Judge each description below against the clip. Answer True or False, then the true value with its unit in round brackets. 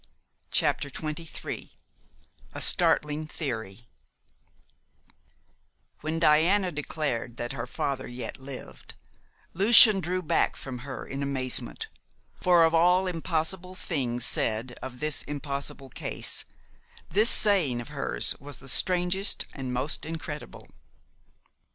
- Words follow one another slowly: True (110 wpm)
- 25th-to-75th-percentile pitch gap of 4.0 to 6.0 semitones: True (5.1 semitones)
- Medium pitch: True (150 Hz)